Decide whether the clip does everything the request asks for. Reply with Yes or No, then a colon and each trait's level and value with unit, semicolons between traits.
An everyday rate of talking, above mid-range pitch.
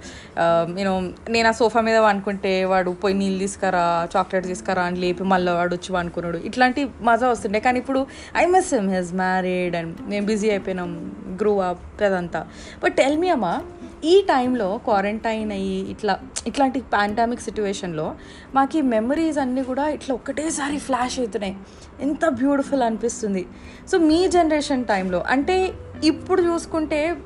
No: fast, 145 wpm; high, 220 Hz